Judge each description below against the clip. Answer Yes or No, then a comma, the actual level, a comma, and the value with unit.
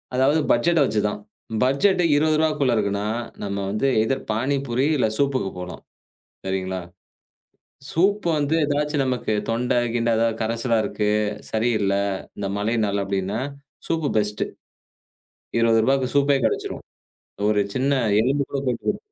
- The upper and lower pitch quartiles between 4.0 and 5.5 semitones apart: Yes, average, 4.8 semitones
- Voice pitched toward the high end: No, low, 120 Hz